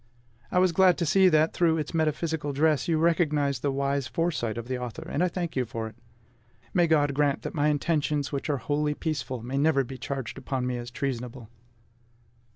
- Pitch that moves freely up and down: No, average, 3.6 semitones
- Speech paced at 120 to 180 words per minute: No, average, 200 wpm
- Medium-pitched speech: Yes, medium, 145 Hz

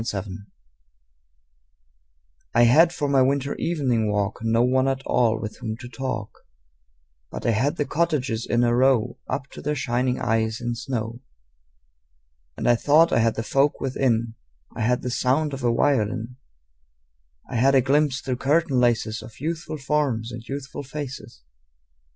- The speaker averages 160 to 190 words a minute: Yes, average, 165 wpm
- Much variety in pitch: No, average, 3.3 semitones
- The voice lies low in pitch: Yes, low, 125 Hz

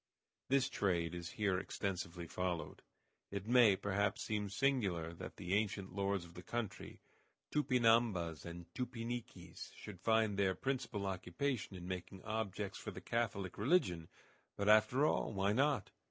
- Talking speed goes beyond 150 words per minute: No, average, 145 wpm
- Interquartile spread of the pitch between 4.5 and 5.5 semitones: No, average, 4.1 semitones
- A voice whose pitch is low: Yes, low, 100 Hz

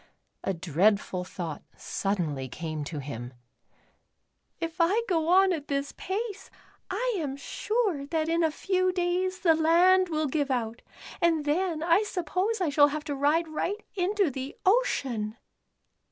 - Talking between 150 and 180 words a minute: Yes, average, 155 wpm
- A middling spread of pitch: No, wide, 6.4 semitones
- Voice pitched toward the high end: Yes, very high, 320 Hz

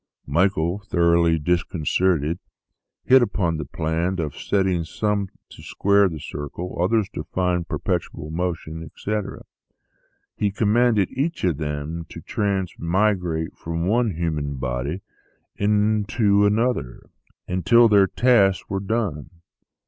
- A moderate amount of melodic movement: Yes, average, 4.0 semitones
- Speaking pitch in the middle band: No, very low, 90 Hz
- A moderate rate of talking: No, slow, 120 wpm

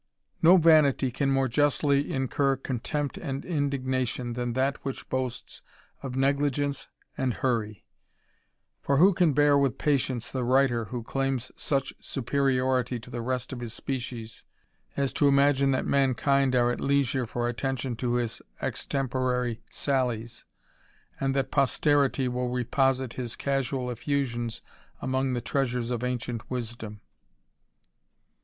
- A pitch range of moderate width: No, narrow, 2.2 semitones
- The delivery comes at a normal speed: No, slow, 130 wpm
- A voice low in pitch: Yes, low, 130 Hz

